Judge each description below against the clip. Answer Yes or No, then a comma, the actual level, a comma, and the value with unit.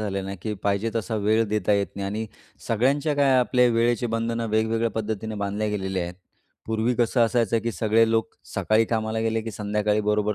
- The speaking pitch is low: Yes, low, 110 Hz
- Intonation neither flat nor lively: No, narrow, 1.6 semitones